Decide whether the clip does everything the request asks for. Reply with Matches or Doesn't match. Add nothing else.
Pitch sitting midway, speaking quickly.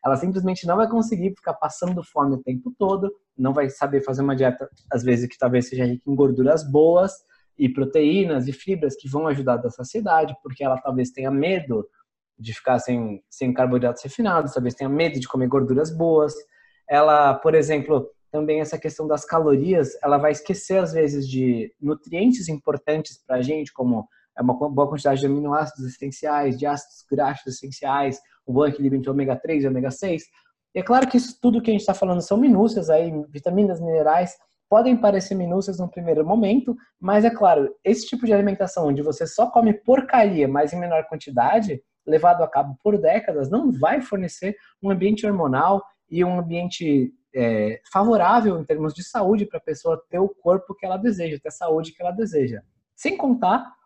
Matches